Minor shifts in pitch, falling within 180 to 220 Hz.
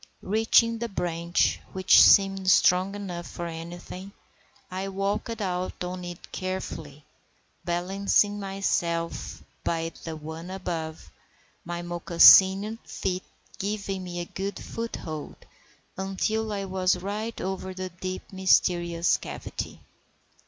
Yes: narrow, 2.3 semitones; medium, 185 Hz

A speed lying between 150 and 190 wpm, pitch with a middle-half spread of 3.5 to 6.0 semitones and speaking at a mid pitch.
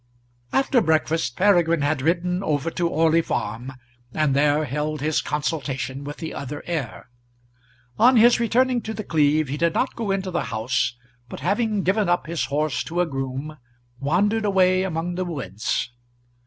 Yes: average, 165 wpm; average, 4.5 semitones; medium, 160 Hz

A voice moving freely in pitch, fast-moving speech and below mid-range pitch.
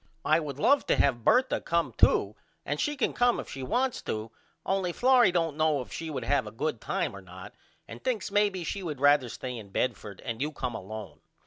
No: wide, 8.4 semitones; fast, 220 wpm; medium, 145 Hz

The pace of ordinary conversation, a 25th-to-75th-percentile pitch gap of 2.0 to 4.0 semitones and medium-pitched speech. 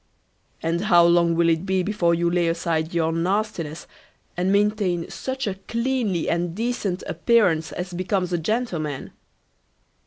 Yes: average, 145 wpm; average, 3.6 semitones; medium, 175 Hz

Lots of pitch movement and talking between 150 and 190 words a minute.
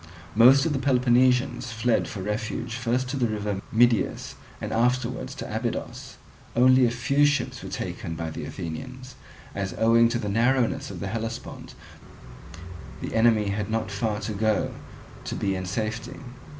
No: average, 3.1 semitones; average, 160 wpm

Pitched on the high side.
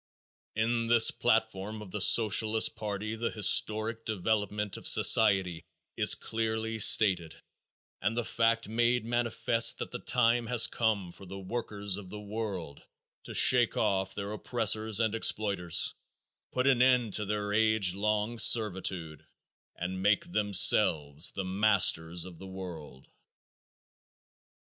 No: low, 105 Hz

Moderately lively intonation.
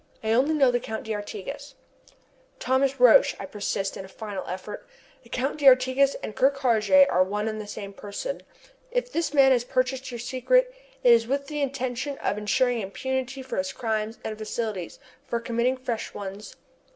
Yes: average, 4.1 semitones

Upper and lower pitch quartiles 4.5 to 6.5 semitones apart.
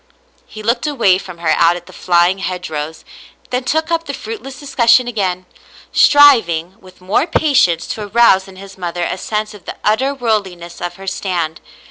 Yes: wide, 5.5 semitones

